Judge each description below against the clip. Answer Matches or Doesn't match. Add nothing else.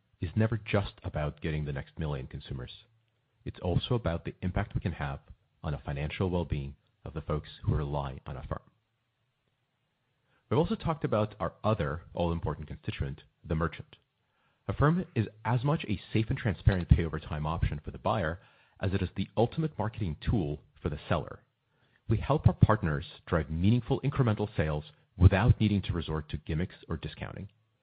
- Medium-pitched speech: Doesn't match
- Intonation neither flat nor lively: Doesn't match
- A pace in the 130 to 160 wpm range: Doesn't match